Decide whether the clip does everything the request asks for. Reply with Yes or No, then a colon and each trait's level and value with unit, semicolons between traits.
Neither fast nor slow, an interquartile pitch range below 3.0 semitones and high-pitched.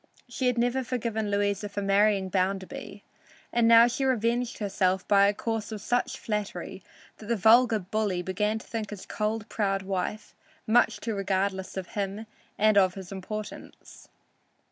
Yes: average, 160 wpm; narrow, 2.4 semitones; high, 210 Hz